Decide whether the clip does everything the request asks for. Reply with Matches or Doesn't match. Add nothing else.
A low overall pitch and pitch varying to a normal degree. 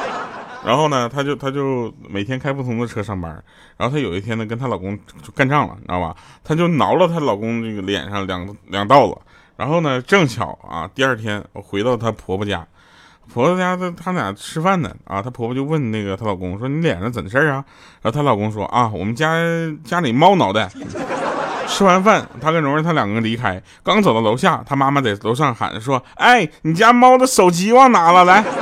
Doesn't match